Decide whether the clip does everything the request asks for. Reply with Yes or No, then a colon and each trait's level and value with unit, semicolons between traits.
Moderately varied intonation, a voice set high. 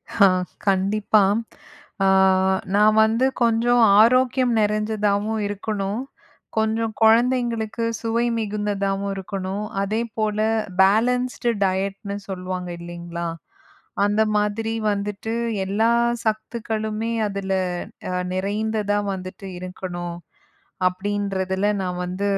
No: narrow, 2.3 semitones; high, 205 Hz